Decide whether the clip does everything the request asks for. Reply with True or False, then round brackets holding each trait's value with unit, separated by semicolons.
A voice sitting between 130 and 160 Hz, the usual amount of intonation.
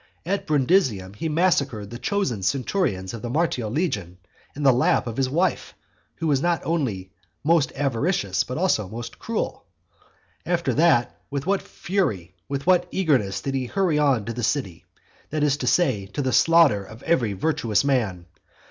False (135 Hz; 7.2 semitones)